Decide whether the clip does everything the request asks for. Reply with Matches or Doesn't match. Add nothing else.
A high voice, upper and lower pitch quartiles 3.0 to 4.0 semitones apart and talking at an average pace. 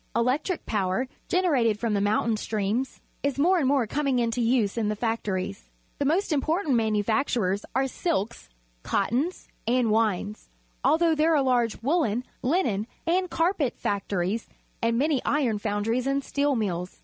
Doesn't match